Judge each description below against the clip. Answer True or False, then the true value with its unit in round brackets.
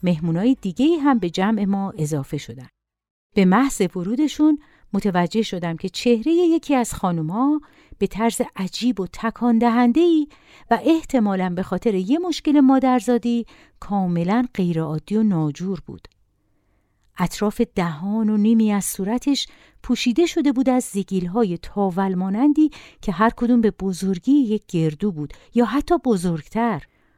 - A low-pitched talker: False (215 Hz)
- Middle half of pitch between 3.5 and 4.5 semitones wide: False (5.3 semitones)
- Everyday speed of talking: True (135 wpm)